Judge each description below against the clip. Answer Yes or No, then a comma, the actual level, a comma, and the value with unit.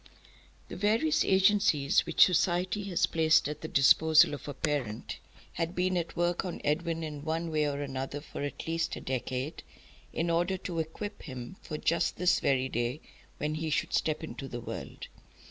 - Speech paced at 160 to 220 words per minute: Yes, average, 180 wpm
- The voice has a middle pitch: Yes, medium, 160 Hz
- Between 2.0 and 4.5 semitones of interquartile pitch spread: Yes, average, 3.4 semitones